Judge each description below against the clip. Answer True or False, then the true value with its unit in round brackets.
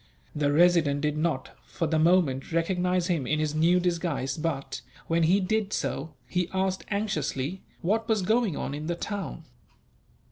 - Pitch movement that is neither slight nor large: True (3.5 semitones)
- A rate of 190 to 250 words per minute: False (165 wpm)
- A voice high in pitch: False (170 Hz)